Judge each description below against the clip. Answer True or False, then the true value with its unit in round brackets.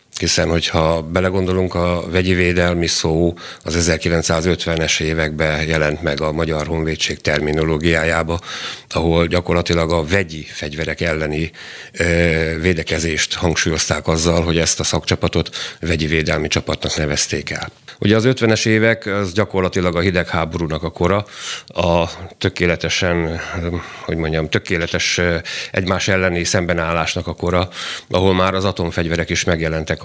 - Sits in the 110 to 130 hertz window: False (85 Hz)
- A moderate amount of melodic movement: False (2.0 semitones)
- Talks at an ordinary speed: True (120 wpm)